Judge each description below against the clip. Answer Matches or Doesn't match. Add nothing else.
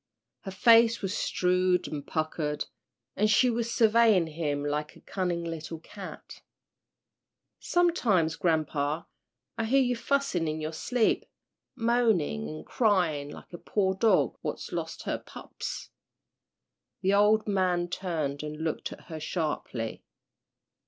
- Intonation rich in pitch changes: Matches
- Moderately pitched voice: Matches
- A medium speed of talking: Doesn't match